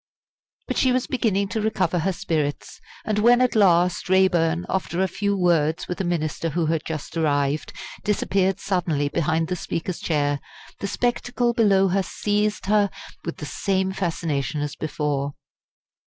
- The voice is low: No, medium, 180 Hz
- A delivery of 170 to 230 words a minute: No, average, 155 wpm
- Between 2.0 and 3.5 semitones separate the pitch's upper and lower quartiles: No, average, 4.1 semitones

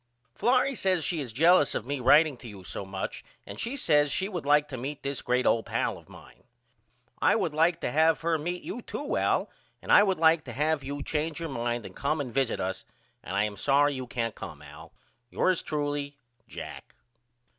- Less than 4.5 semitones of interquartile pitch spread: No, average, 5.0 semitones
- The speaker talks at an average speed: No, fast, 210 wpm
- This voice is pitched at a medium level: Yes, medium, 145 Hz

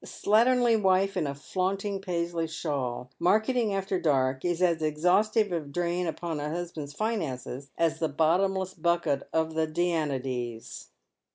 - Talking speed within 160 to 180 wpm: No, average, 145 wpm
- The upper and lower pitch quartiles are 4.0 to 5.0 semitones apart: Yes, average, 4.3 semitones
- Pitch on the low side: No, medium, 170 Hz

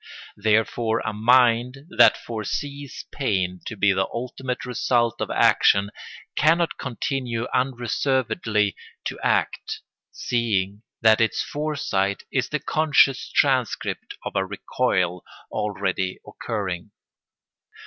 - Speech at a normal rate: No, slow, 105 wpm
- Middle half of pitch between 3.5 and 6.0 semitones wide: Yes, average, 4.2 semitones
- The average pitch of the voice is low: Yes, low, 115 Hz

